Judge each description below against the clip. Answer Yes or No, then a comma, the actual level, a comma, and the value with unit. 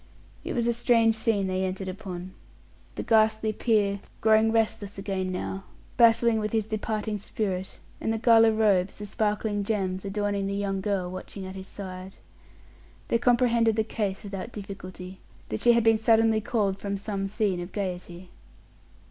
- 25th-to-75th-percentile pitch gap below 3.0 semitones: Yes, narrow, 2.5 semitones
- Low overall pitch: No, high, 205 Hz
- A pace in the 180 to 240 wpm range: No, average, 165 wpm